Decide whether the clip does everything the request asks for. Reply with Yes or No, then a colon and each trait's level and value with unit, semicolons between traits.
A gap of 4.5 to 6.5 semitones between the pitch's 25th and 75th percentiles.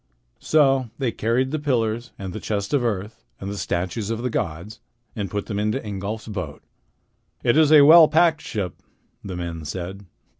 Yes: average, 5.2 semitones